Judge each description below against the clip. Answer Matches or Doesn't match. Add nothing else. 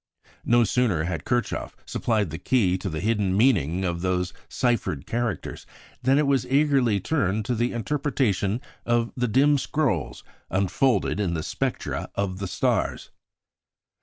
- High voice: Doesn't match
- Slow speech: Doesn't match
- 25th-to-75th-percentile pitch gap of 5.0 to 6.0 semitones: Matches